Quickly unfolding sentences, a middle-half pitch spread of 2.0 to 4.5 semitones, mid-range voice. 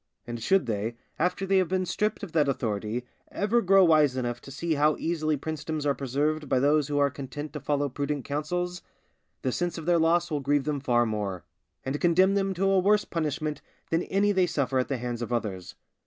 No: fast, 215 wpm; average, 5.0 semitones; medium, 150 Hz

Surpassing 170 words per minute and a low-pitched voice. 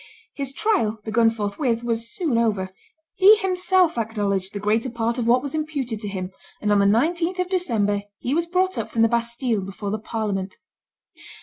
No: average, 185 wpm; high, 230 Hz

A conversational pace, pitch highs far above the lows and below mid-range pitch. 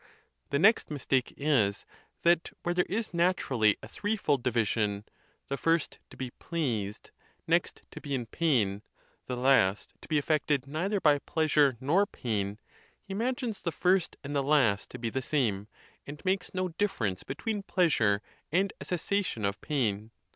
No: average, 155 wpm; wide, 7.5 semitones; medium, 145 Hz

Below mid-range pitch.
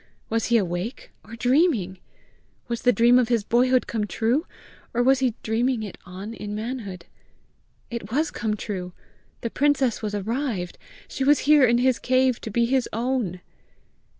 No: high, 235 Hz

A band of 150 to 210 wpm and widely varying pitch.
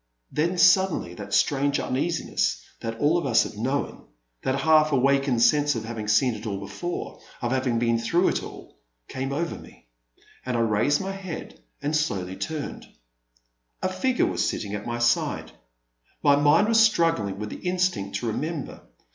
Yes: average, 165 wpm; wide, 6.4 semitones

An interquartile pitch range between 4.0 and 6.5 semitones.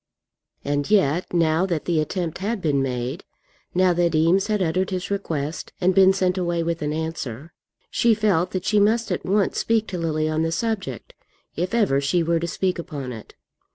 No: average, 3.6 semitones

